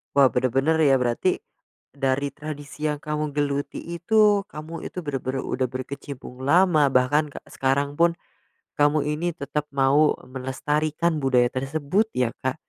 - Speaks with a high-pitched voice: No, medium, 145 Hz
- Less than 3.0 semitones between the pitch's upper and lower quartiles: Yes, narrow, 2.6 semitones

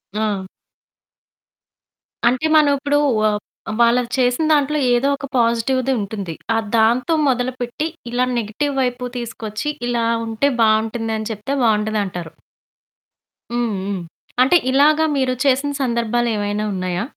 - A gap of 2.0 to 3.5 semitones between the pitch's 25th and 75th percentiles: Yes, average, 3.0 semitones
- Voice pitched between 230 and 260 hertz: Yes, high, 235 Hz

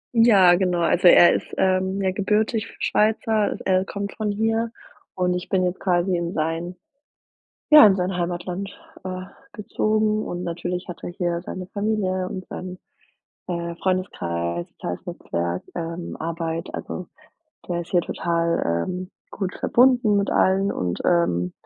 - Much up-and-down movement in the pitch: No, average, 2.7 semitones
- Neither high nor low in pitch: Yes, medium, 180 Hz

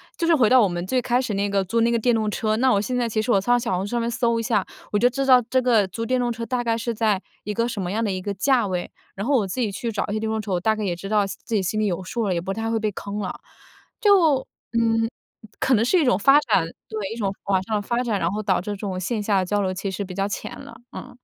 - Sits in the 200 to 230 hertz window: Yes, high, 220 Hz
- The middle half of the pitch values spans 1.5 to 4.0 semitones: Yes, average, 3.3 semitones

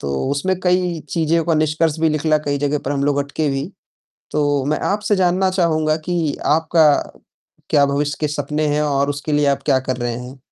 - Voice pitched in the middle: Yes, medium, 150 Hz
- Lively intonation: No, narrow, 2.4 semitones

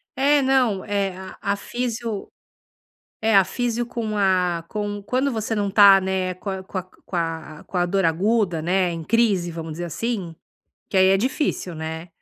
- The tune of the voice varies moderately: Yes, average, 3.9 semitones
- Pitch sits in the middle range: No, high, 195 Hz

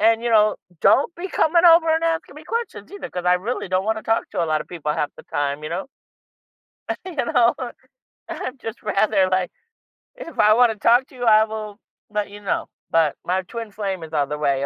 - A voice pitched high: Yes, high, 215 Hz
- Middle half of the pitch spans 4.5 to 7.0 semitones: Yes, wide, 5.4 semitones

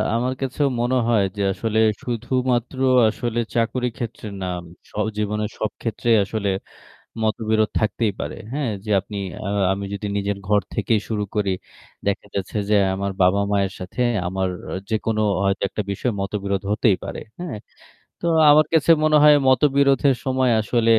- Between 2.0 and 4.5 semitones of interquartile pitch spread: Yes, average, 3.6 semitones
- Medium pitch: No, low, 110 Hz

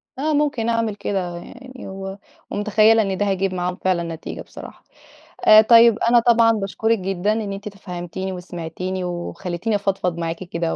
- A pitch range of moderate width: Yes, average, 3.7 semitones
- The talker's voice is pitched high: Yes, high, 195 Hz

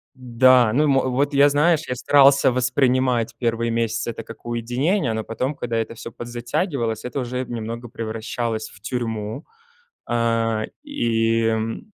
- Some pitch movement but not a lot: No, narrow, 2.3 semitones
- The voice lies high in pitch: No, low, 120 Hz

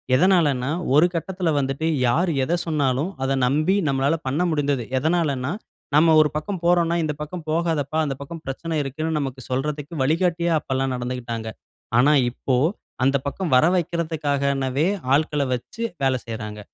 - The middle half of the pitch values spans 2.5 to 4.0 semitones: Yes, average, 3.6 semitones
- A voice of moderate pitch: Yes, medium, 145 Hz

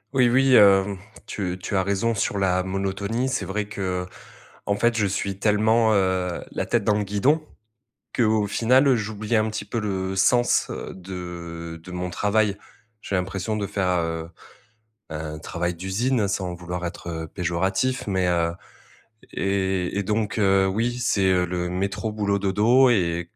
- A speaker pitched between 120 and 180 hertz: No, low, 100 Hz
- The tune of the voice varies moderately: Yes, average, 3.0 semitones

